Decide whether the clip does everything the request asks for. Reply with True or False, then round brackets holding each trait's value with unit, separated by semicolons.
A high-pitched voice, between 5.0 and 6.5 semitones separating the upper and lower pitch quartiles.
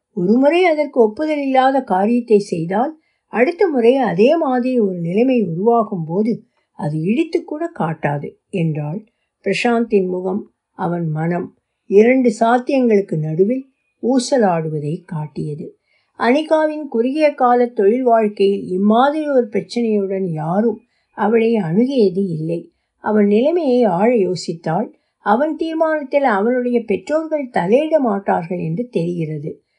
True (225 Hz; 5.6 semitones)